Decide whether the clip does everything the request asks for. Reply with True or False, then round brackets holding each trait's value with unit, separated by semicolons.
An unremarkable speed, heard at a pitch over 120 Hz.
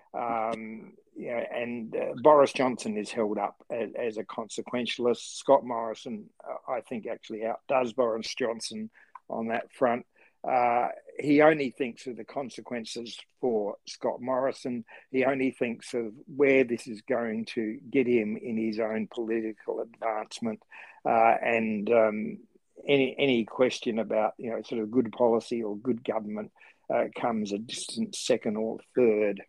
False (150 wpm; 115 Hz)